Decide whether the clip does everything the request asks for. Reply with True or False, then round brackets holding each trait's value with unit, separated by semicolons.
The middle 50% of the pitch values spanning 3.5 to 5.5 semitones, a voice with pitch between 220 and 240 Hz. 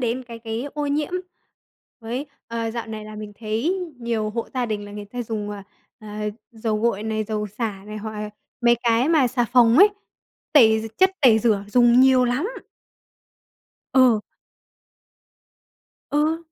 False (2.7 semitones; 230 Hz)